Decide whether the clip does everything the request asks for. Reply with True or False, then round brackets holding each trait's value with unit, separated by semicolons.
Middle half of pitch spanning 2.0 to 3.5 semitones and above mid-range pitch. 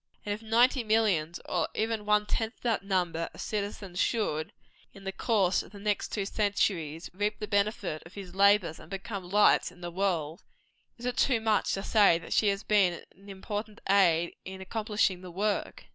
True (2.9 semitones; 200 Hz)